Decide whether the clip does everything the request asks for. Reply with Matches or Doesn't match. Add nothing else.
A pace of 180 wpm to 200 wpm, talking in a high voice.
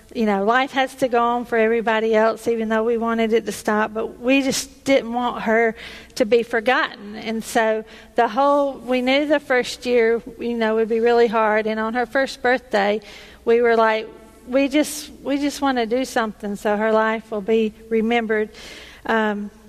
Matches